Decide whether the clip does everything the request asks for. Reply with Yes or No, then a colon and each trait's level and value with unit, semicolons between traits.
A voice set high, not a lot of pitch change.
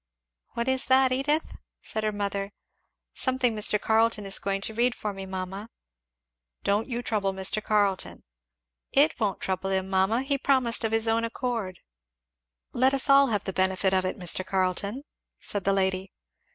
No: high, 210 Hz; average, 4.1 semitones